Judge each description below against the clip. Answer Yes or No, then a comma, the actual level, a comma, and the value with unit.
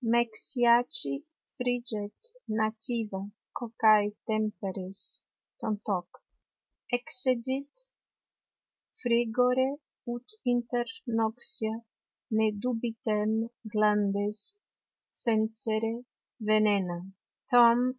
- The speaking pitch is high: Yes, high, 225 Hz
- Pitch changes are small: Yes, narrow, 2.3 semitones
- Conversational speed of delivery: No, slow, 55 wpm